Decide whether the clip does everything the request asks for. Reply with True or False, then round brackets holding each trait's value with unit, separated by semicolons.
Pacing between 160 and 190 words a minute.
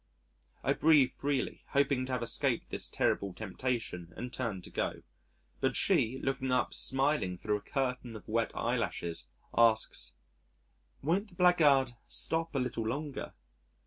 False (145 wpm)